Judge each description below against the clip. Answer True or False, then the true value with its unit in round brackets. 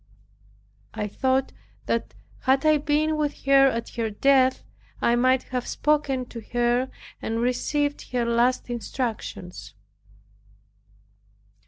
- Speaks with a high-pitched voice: True (255 Hz)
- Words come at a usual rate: False (115 wpm)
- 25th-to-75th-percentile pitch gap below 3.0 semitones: True (2.6 semitones)